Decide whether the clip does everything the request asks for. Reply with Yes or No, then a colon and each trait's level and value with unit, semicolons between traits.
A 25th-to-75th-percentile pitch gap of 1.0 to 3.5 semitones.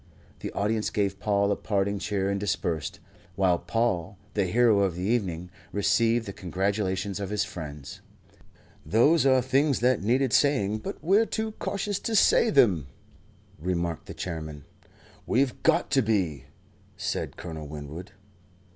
No: average, 5.0 semitones